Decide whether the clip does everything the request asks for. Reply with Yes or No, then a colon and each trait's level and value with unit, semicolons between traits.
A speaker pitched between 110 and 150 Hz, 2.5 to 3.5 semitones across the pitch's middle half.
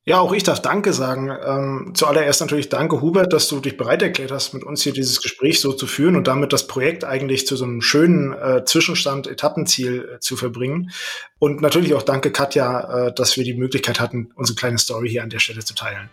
Yes: low, 135 Hz; average, 2.9 semitones